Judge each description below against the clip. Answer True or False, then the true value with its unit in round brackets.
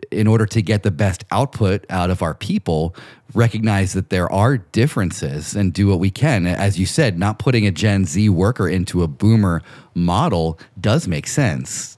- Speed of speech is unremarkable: True (185 wpm)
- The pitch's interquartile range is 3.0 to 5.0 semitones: True (3.3 semitones)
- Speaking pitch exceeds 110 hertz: False (100 Hz)